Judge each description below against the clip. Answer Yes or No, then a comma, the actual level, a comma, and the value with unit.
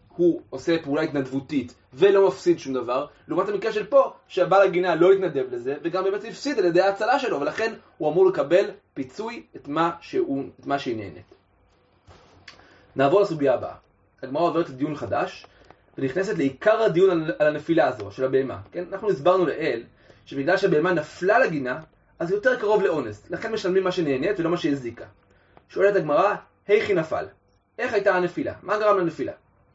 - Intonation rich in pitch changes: Yes, wide, 6.9 semitones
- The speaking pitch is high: No, medium, 175 Hz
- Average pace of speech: No, fast, 160 wpm